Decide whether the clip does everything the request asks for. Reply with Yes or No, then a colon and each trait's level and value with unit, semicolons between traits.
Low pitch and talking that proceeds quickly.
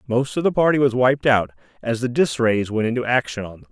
Yes: low, 120 Hz; fast, 260 wpm